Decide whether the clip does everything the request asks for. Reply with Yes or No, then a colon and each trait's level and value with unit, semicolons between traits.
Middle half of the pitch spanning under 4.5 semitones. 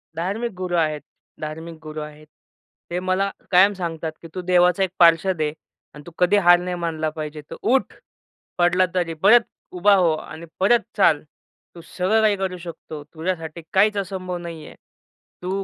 Yes: average, 2.9 semitones